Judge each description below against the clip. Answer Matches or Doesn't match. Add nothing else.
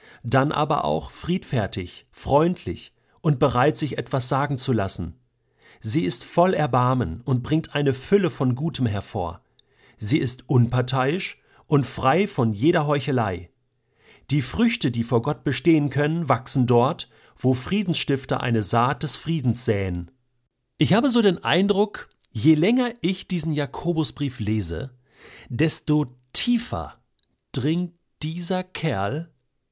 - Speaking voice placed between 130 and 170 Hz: Matches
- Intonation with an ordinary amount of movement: Matches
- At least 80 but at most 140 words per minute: Matches